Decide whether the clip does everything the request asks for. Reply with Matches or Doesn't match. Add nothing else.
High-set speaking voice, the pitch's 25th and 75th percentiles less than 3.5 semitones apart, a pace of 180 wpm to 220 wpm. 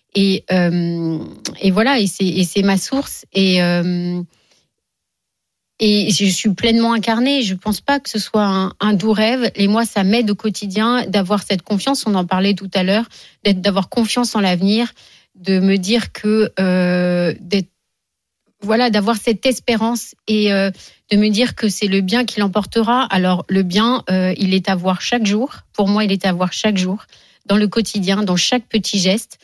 Matches